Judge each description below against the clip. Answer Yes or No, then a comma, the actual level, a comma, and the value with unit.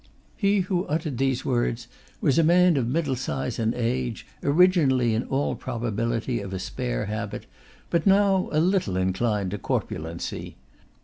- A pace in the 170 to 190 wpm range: No, average, 150 wpm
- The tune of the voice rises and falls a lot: Yes, wide, 6.9 semitones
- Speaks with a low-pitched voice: Yes, low, 125 Hz